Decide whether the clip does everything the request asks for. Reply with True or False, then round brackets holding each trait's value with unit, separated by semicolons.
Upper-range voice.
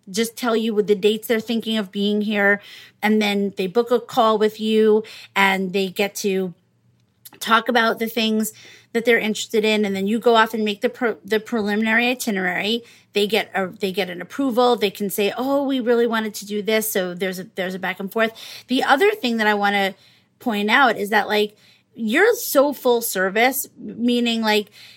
True (215 Hz)